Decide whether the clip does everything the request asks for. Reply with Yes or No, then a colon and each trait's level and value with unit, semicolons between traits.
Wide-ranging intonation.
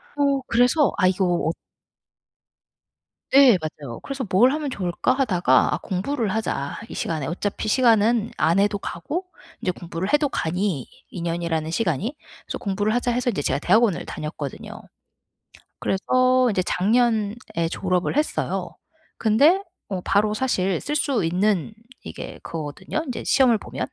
Yes: wide, 6.3 semitones